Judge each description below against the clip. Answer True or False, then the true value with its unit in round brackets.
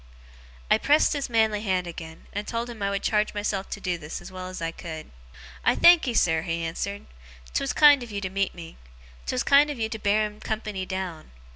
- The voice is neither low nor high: False (200 Hz)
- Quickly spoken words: True (220 wpm)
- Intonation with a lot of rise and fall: False (4.0 semitones)